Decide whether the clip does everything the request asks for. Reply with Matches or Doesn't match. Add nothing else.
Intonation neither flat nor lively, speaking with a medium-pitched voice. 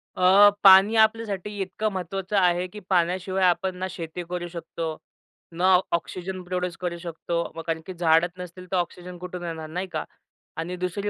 Doesn't match